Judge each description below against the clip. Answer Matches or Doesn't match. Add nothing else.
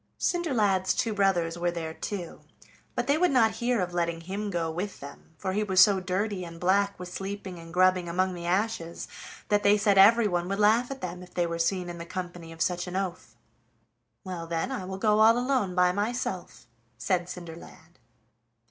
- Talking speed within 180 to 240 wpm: Matches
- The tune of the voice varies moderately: Matches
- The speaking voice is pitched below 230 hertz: Matches